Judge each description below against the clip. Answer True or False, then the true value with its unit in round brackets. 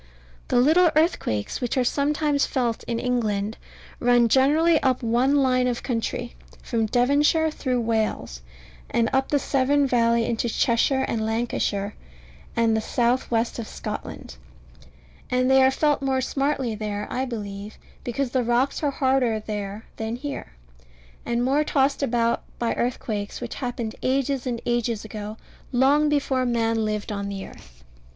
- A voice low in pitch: False (245 Hz)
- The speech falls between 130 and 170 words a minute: True (150 wpm)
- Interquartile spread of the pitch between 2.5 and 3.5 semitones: True (3.1 semitones)